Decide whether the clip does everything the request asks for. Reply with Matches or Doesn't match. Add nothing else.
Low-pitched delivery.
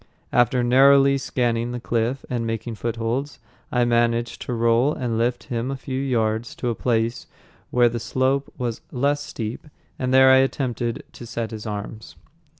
Matches